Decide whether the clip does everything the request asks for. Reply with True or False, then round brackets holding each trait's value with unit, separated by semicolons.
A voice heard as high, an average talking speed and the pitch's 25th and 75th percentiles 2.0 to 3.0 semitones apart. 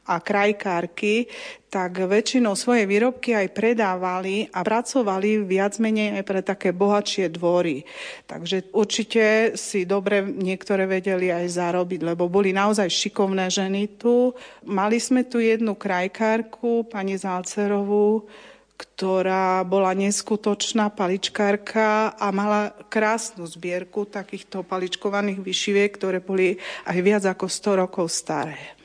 True (200 Hz; 120 wpm; 2.4 semitones)